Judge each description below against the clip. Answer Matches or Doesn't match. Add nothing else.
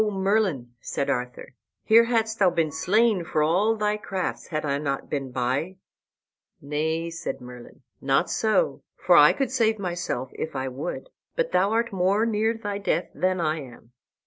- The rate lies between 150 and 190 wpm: Matches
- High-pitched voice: Doesn't match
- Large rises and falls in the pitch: Matches